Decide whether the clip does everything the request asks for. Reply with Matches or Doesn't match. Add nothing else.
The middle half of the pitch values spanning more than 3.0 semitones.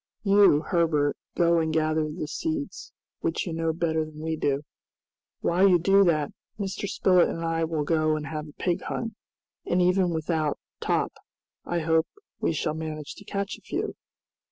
Doesn't match